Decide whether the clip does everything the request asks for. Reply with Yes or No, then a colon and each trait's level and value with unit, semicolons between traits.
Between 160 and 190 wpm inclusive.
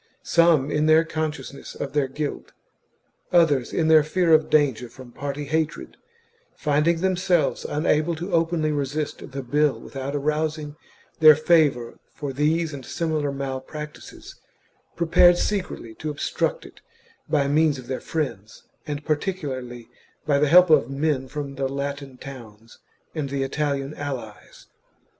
No: average, 140 wpm